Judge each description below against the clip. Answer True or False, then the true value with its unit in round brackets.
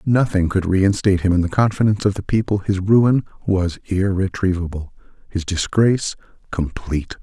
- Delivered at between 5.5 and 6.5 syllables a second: False (5.3 syllables/s)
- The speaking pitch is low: True (95 Hz)